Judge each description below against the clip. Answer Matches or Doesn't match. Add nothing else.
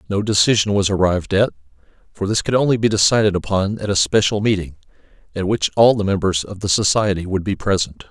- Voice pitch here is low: Matches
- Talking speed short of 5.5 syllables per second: Doesn't match